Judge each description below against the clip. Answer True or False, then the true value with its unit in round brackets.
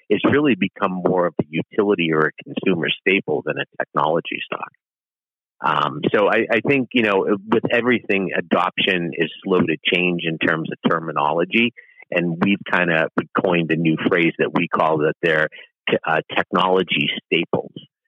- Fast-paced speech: False (165 wpm)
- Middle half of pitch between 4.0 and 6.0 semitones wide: True (4.3 semitones)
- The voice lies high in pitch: False (95 Hz)